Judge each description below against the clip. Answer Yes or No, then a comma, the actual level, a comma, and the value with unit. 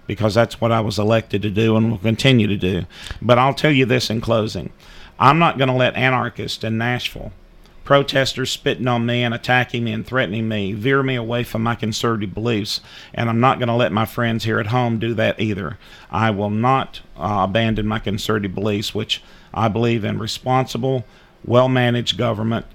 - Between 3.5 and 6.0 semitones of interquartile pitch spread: No, narrow, 2.5 semitones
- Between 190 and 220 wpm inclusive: Yes, average, 200 wpm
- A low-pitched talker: Yes, low, 115 Hz